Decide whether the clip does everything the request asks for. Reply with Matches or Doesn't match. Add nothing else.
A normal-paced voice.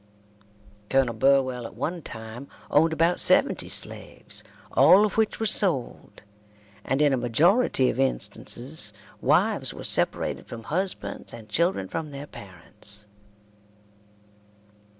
Doesn't match